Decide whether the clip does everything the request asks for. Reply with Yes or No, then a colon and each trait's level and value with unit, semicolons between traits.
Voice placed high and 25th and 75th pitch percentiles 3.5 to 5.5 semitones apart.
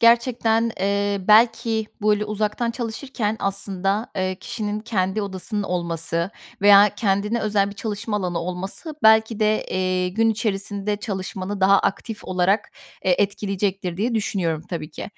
No: high, 205 Hz; narrow, 2.6 semitones